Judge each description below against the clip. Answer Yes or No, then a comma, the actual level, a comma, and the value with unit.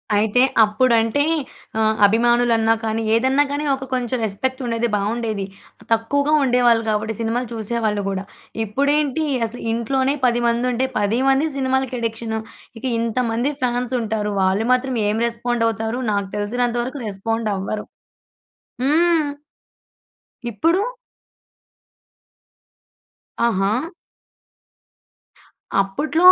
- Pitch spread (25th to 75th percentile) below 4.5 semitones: Yes, average, 3.0 semitones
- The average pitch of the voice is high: Yes, high, 235 Hz